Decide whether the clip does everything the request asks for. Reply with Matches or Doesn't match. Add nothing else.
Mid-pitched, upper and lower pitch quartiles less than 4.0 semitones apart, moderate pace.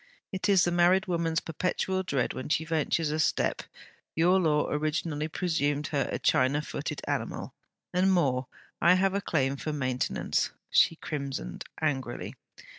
Matches